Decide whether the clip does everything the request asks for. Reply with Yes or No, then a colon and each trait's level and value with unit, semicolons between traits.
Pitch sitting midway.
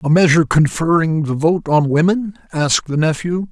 Yes: medium, 165 Hz